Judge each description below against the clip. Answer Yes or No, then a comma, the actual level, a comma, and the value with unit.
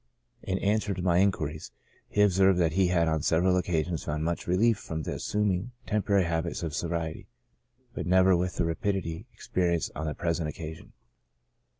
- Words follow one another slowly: No, average, 160 wpm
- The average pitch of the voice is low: Yes, very low, 90 Hz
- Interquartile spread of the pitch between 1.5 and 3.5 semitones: Yes, average, 2.7 semitones